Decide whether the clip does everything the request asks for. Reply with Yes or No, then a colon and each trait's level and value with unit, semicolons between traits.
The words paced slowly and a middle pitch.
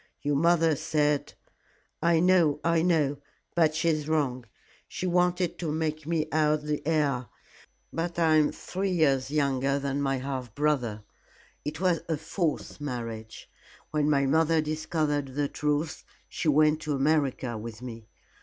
No: average, 155 wpm; medium, 150 Hz